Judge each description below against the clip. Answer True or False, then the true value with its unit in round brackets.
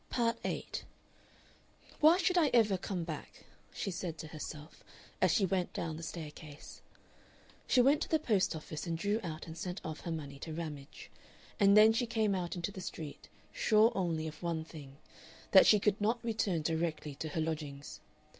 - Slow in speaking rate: False (185 wpm)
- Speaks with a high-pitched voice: False (170 Hz)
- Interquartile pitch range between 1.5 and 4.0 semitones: False (5.1 semitones)